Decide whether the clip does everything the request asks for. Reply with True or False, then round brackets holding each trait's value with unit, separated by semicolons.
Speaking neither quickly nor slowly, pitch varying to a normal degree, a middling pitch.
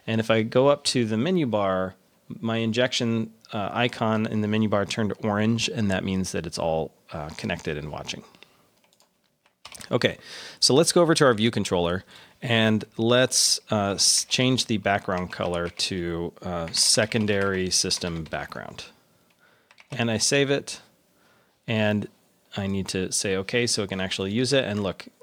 False (160 wpm; 3.6 semitones; 105 Hz)